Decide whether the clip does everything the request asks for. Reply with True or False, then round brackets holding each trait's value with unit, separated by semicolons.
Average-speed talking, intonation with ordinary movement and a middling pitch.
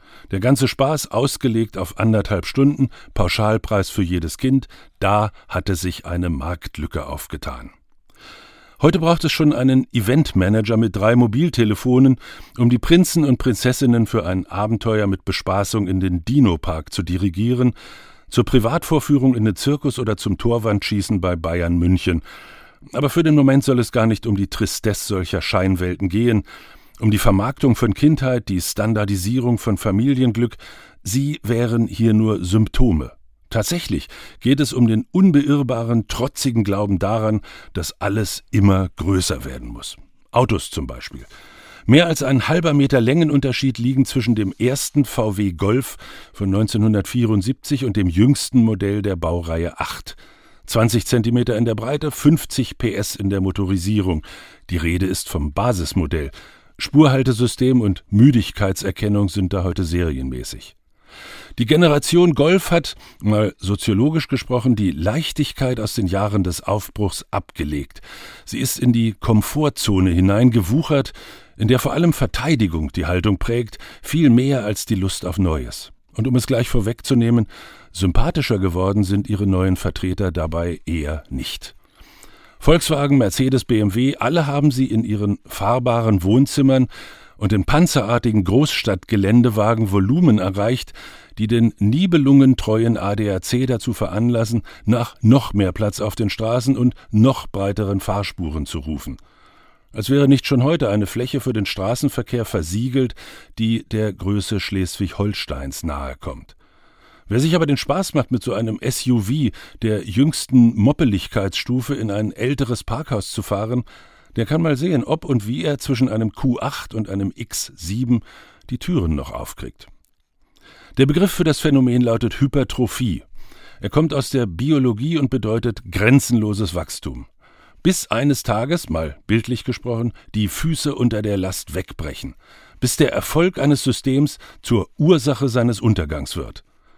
False (140 wpm; 5.0 semitones; 115 Hz)